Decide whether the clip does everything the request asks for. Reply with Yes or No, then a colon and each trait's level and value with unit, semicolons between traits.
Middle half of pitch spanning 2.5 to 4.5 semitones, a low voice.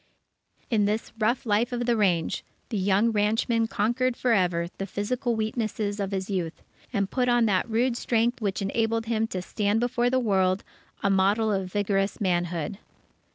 No: average, 3.1 semitones; high, 215 Hz